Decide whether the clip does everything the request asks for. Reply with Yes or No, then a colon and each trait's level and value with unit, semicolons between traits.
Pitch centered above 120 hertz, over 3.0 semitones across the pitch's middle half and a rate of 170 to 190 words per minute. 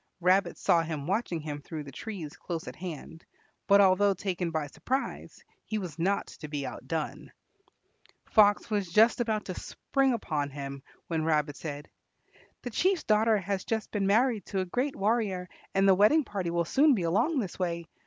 Yes: high, 190 Hz; average, 4.9 semitones; average, 180 wpm